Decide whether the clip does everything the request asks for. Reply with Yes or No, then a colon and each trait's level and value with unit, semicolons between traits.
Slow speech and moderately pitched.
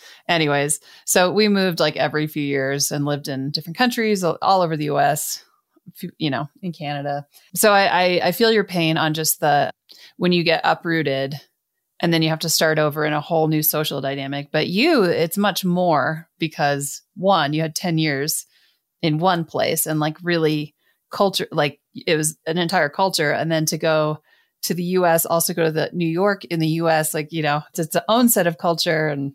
No: fast, 205 wpm; medium, 160 Hz